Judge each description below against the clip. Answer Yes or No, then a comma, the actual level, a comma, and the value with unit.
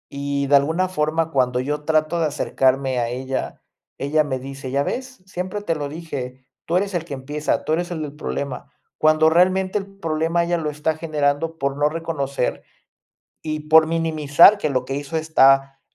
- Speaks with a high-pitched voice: No, medium, 155 Hz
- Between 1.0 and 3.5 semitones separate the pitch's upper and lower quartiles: Yes, average, 3.0 semitones